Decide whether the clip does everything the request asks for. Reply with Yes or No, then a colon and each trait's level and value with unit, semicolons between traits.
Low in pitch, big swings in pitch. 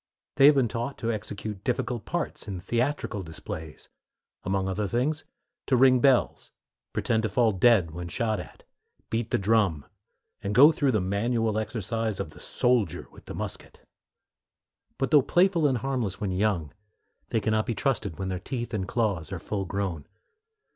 No: low, 110 Hz; average, 4.2 semitones